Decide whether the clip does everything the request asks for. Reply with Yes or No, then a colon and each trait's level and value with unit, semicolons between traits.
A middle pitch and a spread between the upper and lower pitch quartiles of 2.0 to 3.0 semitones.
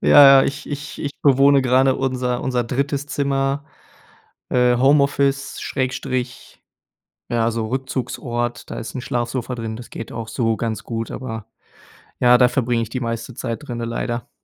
No: low, 125 Hz; narrow, 2.5 semitones